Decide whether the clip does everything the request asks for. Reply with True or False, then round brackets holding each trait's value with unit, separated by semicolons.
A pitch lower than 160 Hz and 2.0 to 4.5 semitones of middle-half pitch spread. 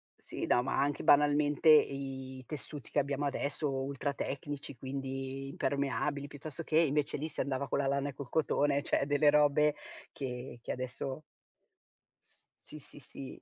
False (140 Hz; 1.5 semitones)